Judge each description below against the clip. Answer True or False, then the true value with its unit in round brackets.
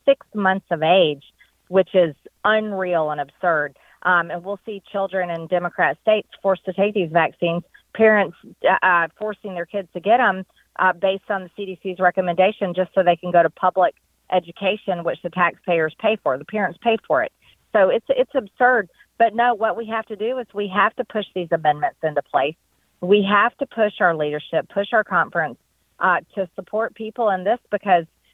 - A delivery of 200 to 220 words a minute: False (190 wpm)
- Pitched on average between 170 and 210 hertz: True (190 Hz)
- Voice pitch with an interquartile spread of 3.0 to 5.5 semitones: True (3.5 semitones)